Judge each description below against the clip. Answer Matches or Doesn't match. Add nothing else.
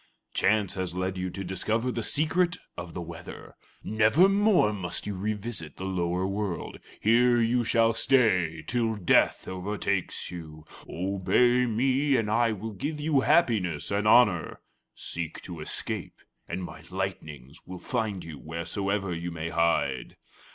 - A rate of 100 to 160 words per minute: Matches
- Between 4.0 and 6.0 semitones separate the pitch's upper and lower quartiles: Matches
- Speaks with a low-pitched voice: Matches